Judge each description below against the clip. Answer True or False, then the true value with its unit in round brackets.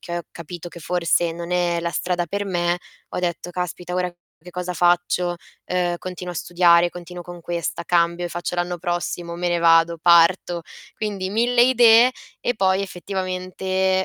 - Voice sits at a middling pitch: True (175 Hz)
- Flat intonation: True (1.2 semitones)